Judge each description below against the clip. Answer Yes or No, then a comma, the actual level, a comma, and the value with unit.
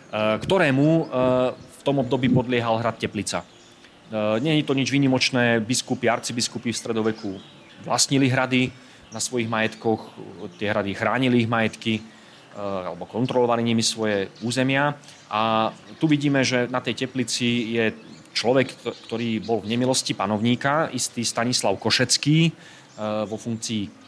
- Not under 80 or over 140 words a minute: Yes, average, 125 wpm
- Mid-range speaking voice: No, low, 120 Hz